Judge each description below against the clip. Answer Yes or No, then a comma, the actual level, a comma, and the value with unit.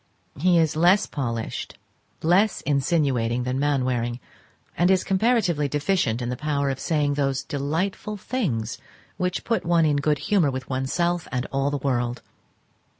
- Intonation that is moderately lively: Yes, average, 5.0 semitones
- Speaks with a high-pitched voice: No, medium, 145 Hz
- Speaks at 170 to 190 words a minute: No, average, 150 wpm